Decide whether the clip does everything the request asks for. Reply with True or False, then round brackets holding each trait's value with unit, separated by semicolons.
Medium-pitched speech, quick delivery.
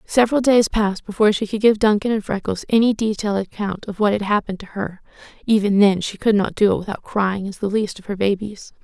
False (205 Hz; 230 wpm)